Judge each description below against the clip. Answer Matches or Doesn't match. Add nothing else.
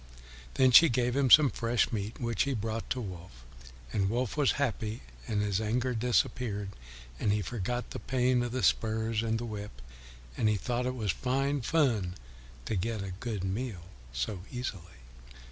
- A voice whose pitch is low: Matches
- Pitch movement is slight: Doesn't match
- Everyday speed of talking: Matches